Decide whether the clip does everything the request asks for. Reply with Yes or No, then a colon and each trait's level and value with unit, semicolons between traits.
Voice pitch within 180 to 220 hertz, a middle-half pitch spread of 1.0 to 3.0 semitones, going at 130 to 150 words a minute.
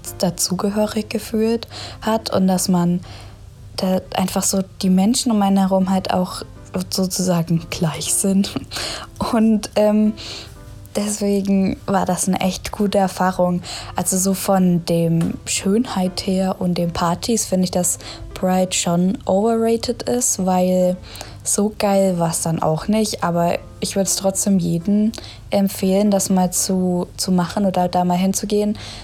Yes: high, 190 Hz; narrow, 2.4 semitones; average, 140 wpm